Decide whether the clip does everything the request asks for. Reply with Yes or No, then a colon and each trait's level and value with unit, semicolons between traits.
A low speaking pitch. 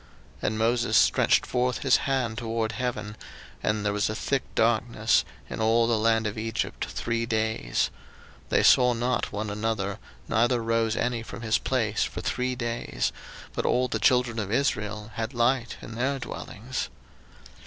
Yes: low, 115 Hz